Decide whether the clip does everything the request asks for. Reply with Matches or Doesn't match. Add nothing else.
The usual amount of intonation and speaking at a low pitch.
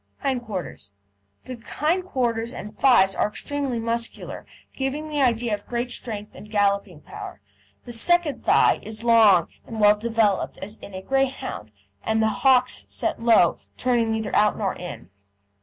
Doesn't match